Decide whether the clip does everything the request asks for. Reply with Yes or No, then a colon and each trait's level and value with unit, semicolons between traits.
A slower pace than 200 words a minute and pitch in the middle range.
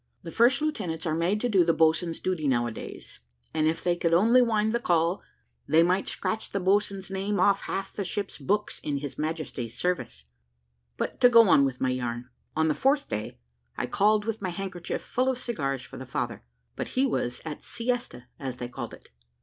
No: fast, 205 wpm; medium, 175 Hz